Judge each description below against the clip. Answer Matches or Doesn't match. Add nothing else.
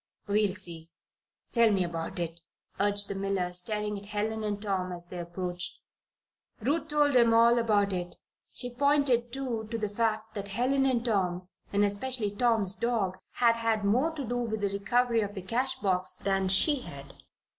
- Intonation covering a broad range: Doesn't match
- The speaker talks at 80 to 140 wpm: Doesn't match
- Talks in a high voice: Matches